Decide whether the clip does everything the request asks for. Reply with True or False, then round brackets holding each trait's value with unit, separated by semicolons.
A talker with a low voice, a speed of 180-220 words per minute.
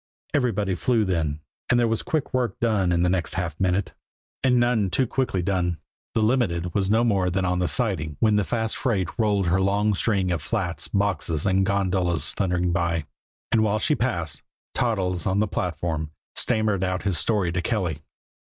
True (95 Hz; 185 wpm)